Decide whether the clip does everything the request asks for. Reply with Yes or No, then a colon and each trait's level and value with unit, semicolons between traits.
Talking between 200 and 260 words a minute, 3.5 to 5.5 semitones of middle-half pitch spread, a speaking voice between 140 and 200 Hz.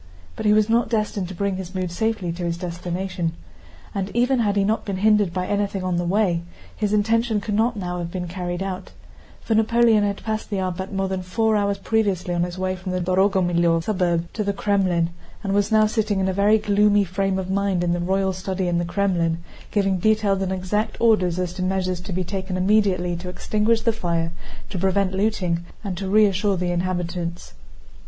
No: fast, 205 wpm; narrow, 2.6 semitones; high, 190 Hz